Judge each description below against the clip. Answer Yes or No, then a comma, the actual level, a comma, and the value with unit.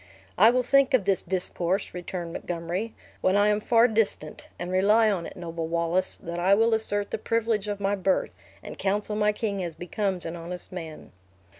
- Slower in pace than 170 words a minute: No, average, 190 wpm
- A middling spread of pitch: Yes, average, 3.4 semitones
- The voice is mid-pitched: No, high, 195 Hz